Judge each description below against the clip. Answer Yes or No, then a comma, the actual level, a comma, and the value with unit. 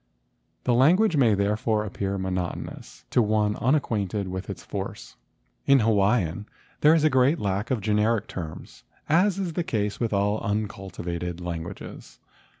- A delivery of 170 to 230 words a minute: No, average, 150 wpm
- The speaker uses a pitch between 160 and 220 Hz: No, low, 105 Hz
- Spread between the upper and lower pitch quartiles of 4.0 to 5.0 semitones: Yes, average, 4.5 semitones